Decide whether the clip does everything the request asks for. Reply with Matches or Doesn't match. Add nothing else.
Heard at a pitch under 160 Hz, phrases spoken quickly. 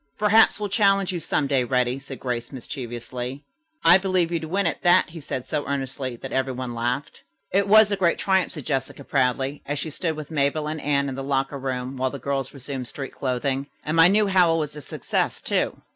Matches